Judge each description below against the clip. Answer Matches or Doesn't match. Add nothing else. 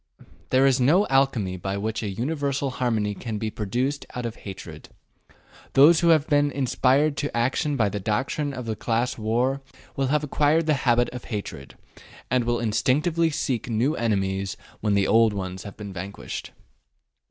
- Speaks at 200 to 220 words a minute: Doesn't match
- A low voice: Matches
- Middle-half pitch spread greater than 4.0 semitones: Matches